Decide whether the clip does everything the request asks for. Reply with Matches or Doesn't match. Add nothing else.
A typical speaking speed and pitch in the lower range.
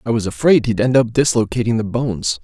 Doesn't match